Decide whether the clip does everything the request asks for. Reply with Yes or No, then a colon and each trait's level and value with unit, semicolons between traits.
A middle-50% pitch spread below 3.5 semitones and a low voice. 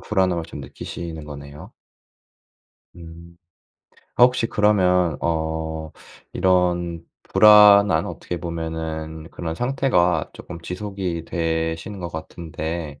Yes: narrow, 2.5 semitones; very low, 85 Hz